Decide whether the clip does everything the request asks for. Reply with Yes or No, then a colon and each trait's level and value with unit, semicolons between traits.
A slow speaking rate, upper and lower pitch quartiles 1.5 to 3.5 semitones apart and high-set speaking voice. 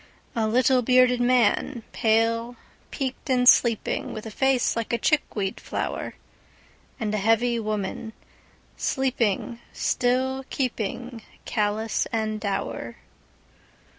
Yes: slow, 95 wpm; narrow, 2.6 semitones; high, 230 Hz